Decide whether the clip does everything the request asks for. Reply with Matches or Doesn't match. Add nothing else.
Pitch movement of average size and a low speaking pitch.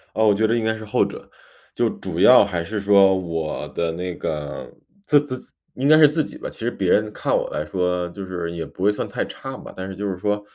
Matches